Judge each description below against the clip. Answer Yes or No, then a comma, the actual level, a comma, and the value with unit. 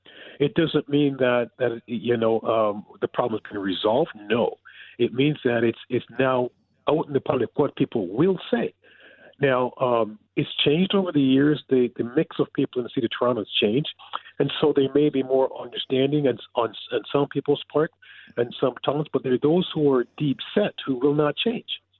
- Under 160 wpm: No, fast, 205 wpm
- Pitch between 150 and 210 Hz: No, low, 135 Hz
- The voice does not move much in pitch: No, average, 3.2 semitones